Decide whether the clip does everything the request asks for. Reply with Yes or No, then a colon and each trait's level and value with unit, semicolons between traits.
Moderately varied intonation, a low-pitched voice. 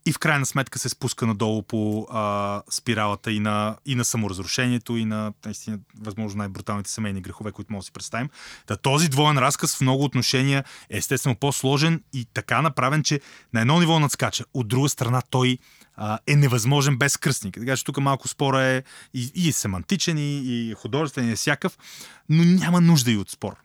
Yes: average, 4.7 semitones; low, 125 Hz